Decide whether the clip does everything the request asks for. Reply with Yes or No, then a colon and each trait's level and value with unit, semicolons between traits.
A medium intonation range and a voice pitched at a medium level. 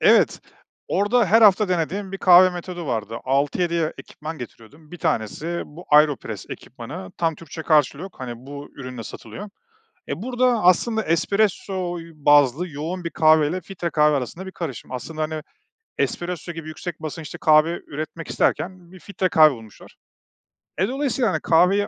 Yes: average, 3.7 semitones; medium, 165 Hz